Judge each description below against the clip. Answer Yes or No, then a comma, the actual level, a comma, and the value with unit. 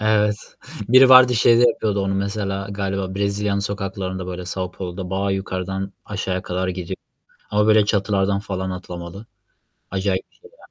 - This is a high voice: No, low, 100 Hz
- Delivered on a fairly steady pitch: Yes, narrow, 1.8 semitones